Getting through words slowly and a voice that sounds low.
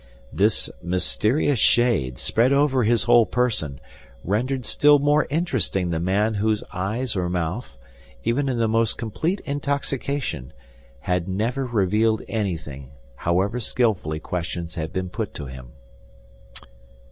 Yes: slow, 125 wpm; low, 110 Hz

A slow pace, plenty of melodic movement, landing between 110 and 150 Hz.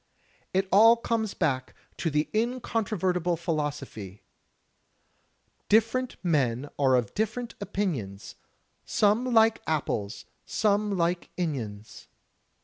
No: slow, 95 wpm; wide, 8.0 semitones; medium, 180 Hz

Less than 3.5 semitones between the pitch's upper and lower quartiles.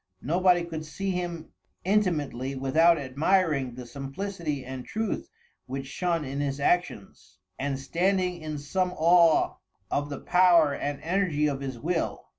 No: average, 4.5 semitones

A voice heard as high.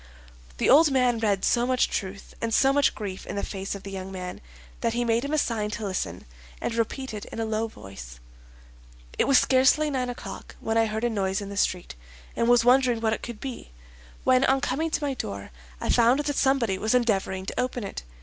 Yes: high, 230 Hz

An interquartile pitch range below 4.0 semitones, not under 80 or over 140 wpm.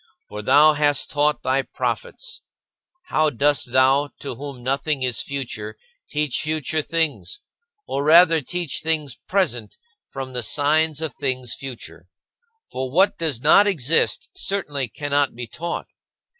Yes: average, 3.3 semitones; slow, 135 wpm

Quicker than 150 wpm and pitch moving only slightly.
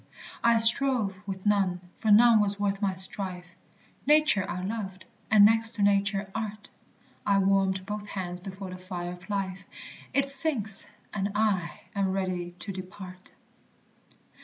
No: average, 145 wpm; narrow, 2.3 semitones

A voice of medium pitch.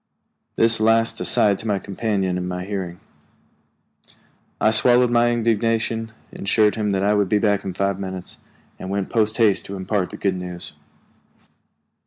No: low, 105 Hz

